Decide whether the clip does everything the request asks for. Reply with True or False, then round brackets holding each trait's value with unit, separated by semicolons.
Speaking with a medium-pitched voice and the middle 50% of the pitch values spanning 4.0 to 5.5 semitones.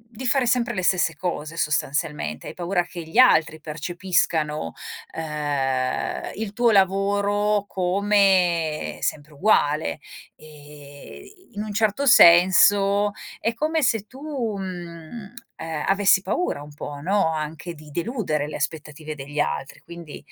True (175 Hz; 5.1 semitones)